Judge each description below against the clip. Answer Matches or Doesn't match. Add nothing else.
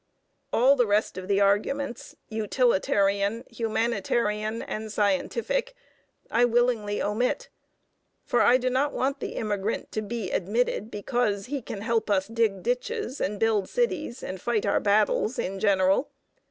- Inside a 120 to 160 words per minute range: Matches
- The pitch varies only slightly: Doesn't match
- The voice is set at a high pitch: Matches